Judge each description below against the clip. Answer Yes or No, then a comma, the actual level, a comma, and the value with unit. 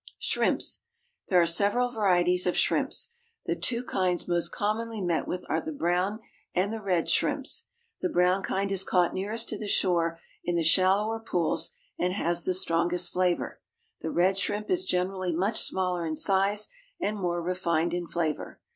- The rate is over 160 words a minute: Yes, average, 170 wpm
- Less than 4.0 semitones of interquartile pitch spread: Yes, average, 2.8 semitones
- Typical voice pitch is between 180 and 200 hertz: Yes, medium, 185 Hz